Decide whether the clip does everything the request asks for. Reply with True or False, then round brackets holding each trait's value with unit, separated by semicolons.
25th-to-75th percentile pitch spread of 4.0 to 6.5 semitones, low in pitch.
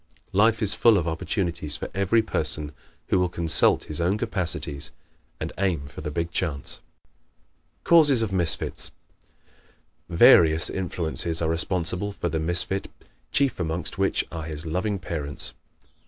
False (3.5 semitones; 85 Hz)